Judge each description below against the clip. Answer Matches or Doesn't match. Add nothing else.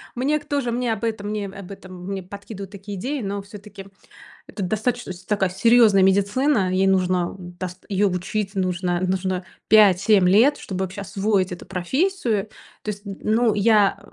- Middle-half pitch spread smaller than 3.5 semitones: Matches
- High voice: Matches